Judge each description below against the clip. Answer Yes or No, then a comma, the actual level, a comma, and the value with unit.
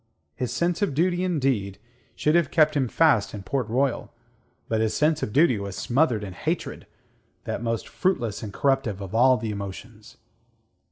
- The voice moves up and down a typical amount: No, wide, 6.4 semitones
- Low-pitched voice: Yes, low, 125 Hz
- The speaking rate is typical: Yes, average, 170 wpm